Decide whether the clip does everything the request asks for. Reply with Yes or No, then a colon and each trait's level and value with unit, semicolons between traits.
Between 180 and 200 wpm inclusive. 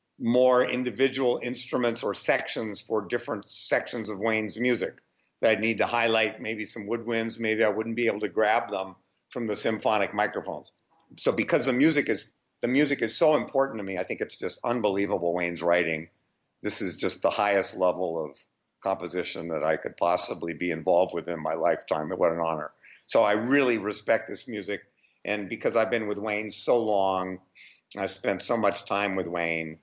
Yes: average, 185 wpm